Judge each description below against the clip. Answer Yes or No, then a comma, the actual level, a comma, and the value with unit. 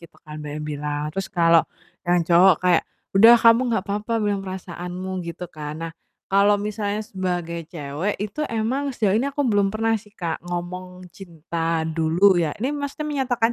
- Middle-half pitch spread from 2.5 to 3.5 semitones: No, average, 4.0 semitones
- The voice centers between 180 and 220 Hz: Yes, medium, 185 Hz